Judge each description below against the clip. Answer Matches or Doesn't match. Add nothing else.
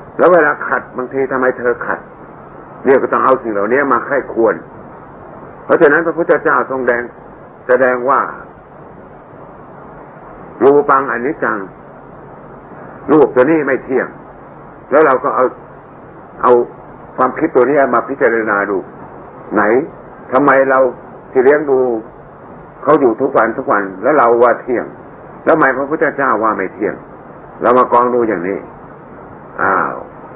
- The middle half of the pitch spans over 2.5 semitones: Doesn't match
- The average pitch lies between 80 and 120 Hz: Doesn't match